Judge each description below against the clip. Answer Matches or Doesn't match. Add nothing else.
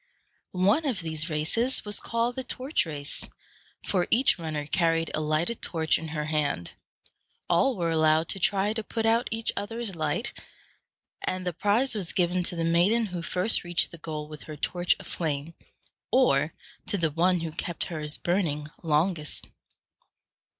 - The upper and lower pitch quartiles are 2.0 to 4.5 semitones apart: Doesn't match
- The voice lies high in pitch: Doesn't match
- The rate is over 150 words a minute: Matches